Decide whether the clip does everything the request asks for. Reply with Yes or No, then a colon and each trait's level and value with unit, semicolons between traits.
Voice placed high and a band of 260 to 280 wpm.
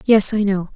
No: high, 200 Hz; fast, 240 wpm